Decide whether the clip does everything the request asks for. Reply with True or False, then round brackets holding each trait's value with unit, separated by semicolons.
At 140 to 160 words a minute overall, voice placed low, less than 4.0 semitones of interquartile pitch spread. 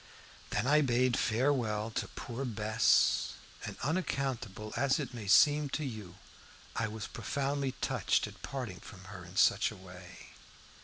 False (150 wpm; 120 Hz; 4.6 semitones)